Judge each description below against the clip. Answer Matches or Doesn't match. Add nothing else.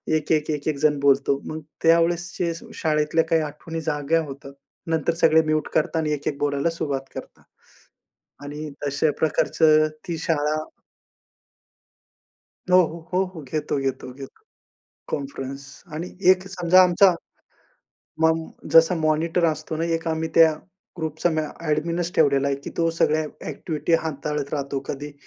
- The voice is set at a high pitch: Doesn't match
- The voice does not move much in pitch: Matches